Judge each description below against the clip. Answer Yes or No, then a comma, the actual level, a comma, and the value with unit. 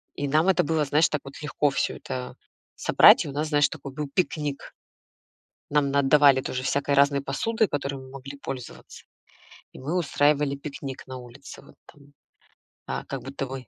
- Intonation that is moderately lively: No, narrow, 1.5 semitones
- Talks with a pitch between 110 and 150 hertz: Yes, medium, 140 Hz